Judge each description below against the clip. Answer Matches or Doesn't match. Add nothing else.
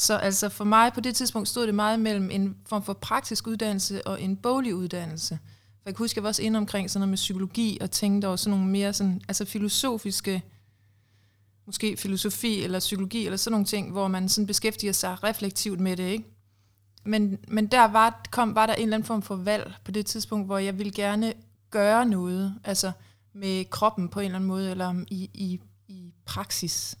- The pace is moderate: Matches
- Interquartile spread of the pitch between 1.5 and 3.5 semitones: Matches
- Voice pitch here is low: Doesn't match